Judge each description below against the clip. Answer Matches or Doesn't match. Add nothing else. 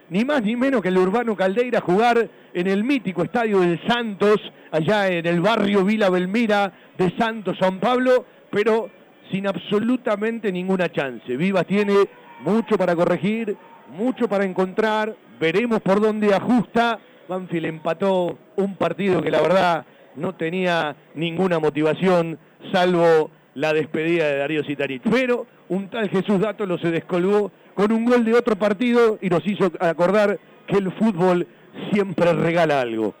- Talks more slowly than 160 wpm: Matches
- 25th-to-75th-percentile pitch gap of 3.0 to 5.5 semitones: Matches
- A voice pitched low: Doesn't match